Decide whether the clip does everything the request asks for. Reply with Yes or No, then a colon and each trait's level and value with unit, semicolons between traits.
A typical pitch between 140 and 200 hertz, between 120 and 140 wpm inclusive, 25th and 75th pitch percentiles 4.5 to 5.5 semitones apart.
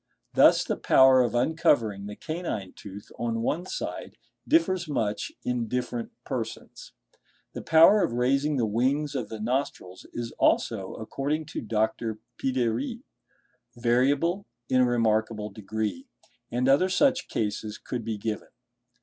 No: low, 125 Hz; slow, 135 wpm; average, 5.2 semitones